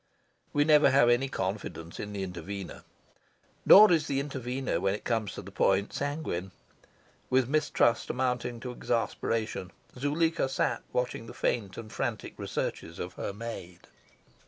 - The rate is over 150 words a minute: No, average, 145 wpm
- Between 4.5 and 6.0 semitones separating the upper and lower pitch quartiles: Yes, wide, 5.6 semitones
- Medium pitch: No, low, 120 Hz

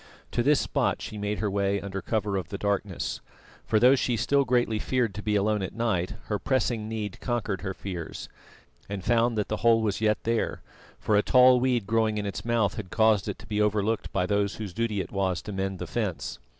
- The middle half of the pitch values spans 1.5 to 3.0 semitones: Yes, narrow, 2.5 semitones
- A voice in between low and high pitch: No, low, 105 Hz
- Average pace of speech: No, fast, 220 wpm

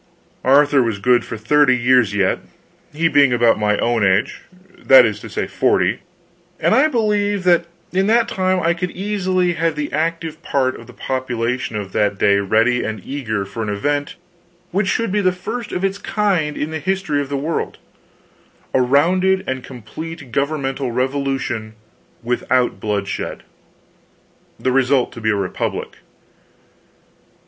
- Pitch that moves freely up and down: Yes, wide, 6.9 semitones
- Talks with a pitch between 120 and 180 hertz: Yes, medium, 140 Hz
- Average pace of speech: Yes, average, 155 wpm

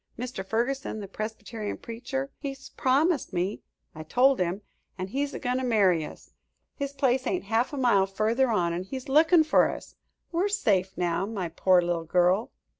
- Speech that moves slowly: No, average, 180 wpm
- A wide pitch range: Yes, wide, 6.1 semitones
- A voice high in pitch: Yes, high, 225 Hz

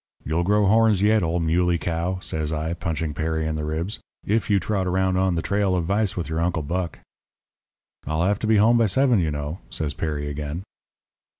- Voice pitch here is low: Yes, very low, 85 Hz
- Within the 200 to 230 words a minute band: Yes, fast, 205 wpm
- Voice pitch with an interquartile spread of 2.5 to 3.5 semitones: No, average, 4.0 semitones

